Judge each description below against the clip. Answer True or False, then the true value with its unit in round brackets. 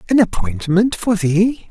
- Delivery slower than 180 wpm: True (140 wpm)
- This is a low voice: False (195 Hz)